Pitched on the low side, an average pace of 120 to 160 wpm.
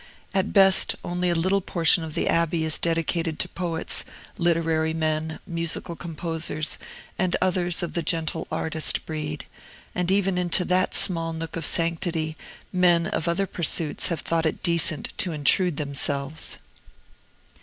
No: medium, 165 Hz; average, 145 wpm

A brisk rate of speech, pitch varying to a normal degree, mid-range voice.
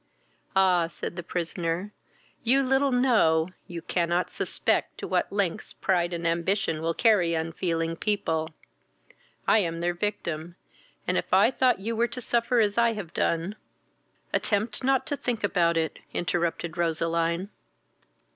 No: average, 145 wpm; average, 4.6 semitones; medium, 175 Hz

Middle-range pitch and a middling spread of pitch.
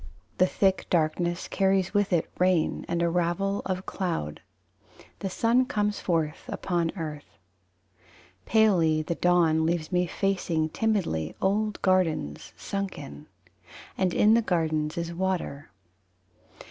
Yes: medium, 175 Hz; average, 3.3 semitones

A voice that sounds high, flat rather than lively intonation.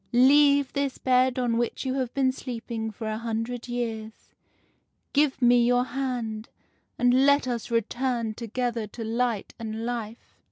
Yes: high, 240 Hz; narrow, 2.2 semitones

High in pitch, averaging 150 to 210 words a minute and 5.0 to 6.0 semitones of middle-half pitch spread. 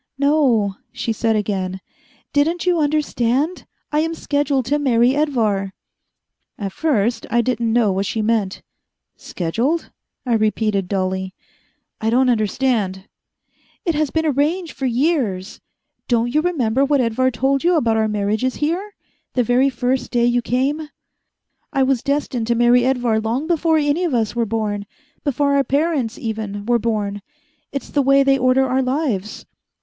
No: high, 245 Hz; average, 155 wpm; average, 4.6 semitones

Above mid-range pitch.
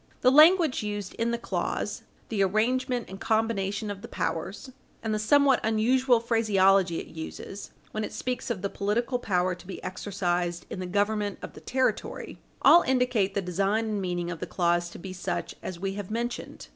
Yes: high, 205 Hz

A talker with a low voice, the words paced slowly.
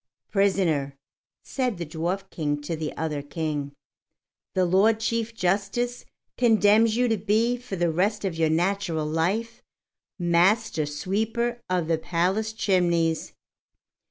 No: medium, 185 Hz; slow, 130 wpm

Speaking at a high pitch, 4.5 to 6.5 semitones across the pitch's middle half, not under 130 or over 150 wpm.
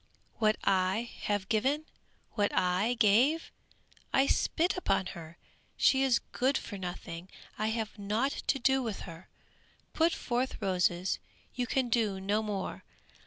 Yes: high, 215 Hz; average, 5.3 semitones; average, 140 wpm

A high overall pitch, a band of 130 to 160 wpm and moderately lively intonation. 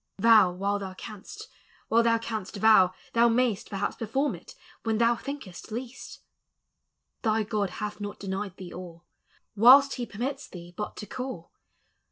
Yes: high, 215 Hz; average, 155 wpm; average, 3.4 semitones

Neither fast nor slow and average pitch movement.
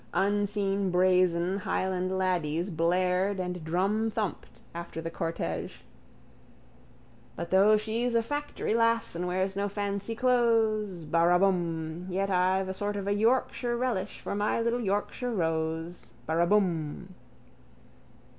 No: slow, 120 wpm; average, 3.1 semitones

